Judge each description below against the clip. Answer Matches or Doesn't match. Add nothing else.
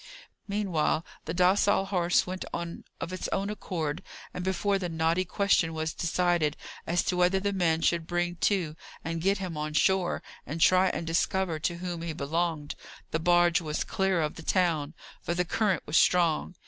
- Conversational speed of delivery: Matches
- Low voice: Doesn't match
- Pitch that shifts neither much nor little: Doesn't match